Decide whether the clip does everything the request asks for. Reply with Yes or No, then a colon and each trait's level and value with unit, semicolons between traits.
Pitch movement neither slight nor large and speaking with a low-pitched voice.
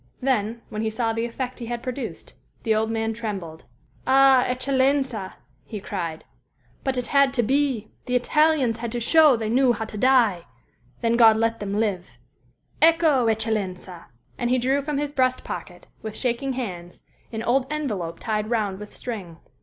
No: average, 3.6 semitones; high, 235 Hz